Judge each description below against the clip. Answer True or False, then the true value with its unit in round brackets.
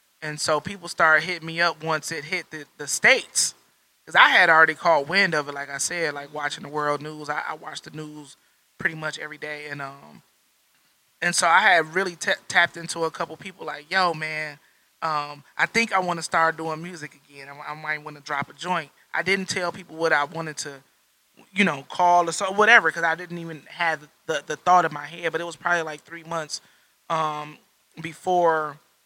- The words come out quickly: True (220 wpm)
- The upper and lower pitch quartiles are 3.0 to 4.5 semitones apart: False (2.6 semitones)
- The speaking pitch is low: False (160 Hz)